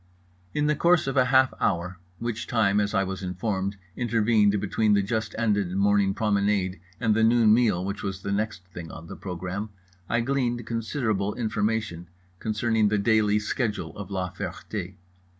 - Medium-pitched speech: No, low, 105 Hz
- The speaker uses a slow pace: No, average, 170 wpm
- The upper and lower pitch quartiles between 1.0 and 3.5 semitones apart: Yes, average, 2.8 semitones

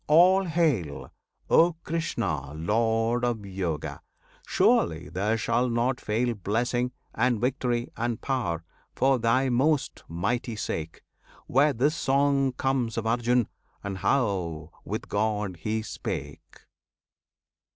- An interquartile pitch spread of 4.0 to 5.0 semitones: Yes, average, 4.5 semitones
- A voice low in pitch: Yes, low, 120 Hz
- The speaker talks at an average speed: No, slow, 115 wpm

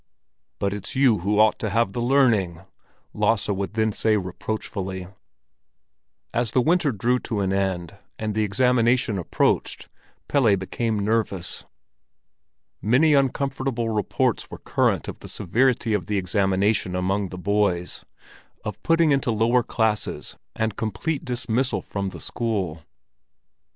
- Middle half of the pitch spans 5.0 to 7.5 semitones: No, average, 3.9 semitones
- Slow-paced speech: Yes, slow, 130 wpm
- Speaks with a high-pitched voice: No, low, 110 Hz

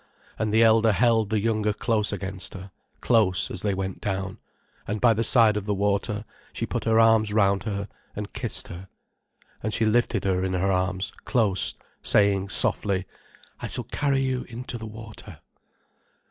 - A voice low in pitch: Yes, low, 105 Hz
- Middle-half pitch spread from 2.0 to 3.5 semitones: Yes, narrow, 2.5 semitones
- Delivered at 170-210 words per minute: Yes, average, 175 wpm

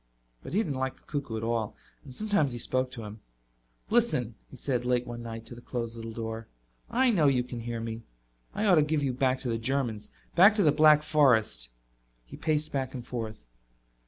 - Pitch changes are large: No, average, 4.6 semitones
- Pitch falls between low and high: No, low, 125 Hz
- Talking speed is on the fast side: Yes, fast, 215 wpm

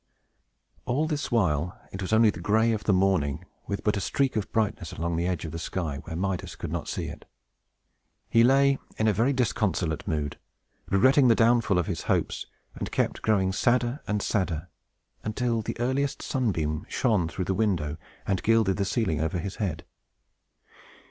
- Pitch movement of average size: Yes, average, 5.0 semitones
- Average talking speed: Yes, average, 180 wpm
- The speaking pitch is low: Yes, low, 100 Hz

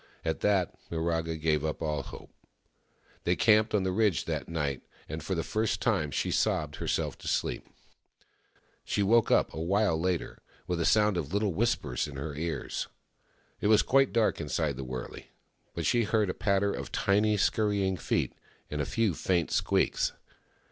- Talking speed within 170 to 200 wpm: Yes, average, 175 wpm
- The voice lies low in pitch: Yes, very low, 90 Hz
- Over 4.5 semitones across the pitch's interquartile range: Yes, average, 4.9 semitones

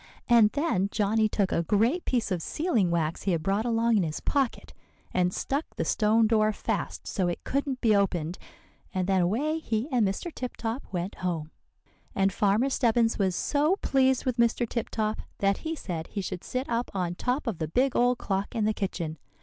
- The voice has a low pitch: No, high, 215 Hz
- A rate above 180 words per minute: Yes, average, 200 wpm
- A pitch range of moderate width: Yes, average, 4.9 semitones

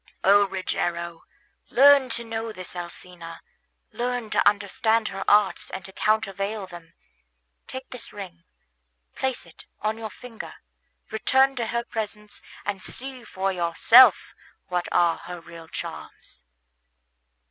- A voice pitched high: Yes, high, 205 Hz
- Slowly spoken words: Yes, slow, 125 wpm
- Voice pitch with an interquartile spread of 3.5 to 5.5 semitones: Yes, average, 4.4 semitones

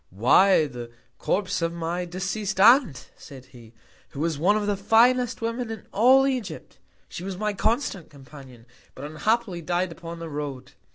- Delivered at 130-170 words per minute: Yes, average, 165 wpm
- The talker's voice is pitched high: No, medium, 180 Hz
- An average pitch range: No, wide, 6.5 semitones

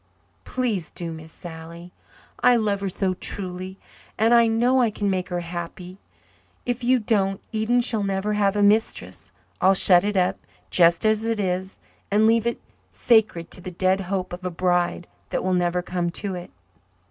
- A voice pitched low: No, high, 190 Hz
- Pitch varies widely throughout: No, average, 3.5 semitones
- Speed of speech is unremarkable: Yes, average, 180 wpm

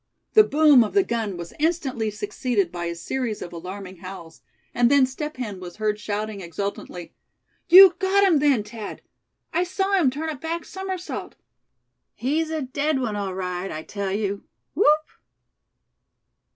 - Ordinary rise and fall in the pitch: No, wide, 7.9 semitones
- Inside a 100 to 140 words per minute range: No, average, 160 wpm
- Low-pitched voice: No, high, 235 Hz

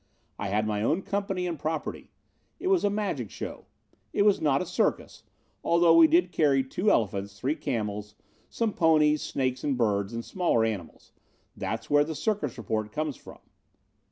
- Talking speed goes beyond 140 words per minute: Yes, average, 170 wpm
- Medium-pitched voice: Yes, medium, 145 Hz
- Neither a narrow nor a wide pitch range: No, wide, 8.0 semitones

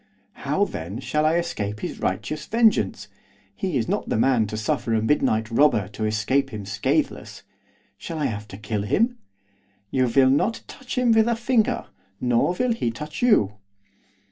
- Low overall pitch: Yes, low, 130 Hz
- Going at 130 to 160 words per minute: No, average, 170 wpm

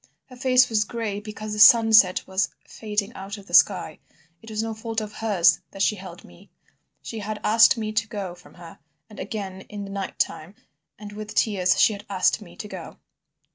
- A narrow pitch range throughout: Yes, narrow, 2.1 semitones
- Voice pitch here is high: Yes, high, 210 Hz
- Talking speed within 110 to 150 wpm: No, fast, 205 wpm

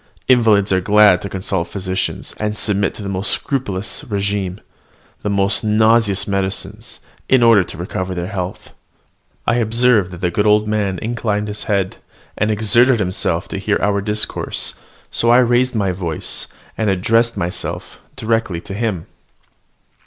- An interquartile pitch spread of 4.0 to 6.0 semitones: No, average, 2.8 semitones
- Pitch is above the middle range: No, low, 105 Hz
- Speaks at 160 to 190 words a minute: No, average, 150 wpm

